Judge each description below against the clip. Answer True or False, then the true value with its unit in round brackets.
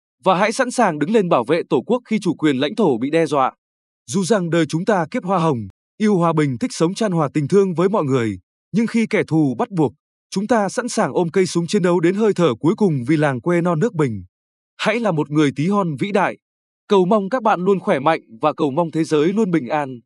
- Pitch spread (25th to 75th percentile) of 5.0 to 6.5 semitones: True (5.5 semitones)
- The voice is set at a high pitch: False (170 Hz)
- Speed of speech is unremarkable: False (260 wpm)